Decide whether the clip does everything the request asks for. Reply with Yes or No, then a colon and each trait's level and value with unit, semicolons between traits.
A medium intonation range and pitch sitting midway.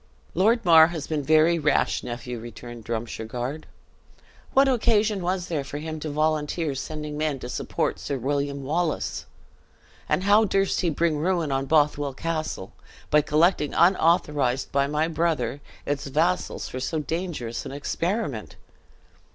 Yes: average, 3.7 semitones; medium, 150 Hz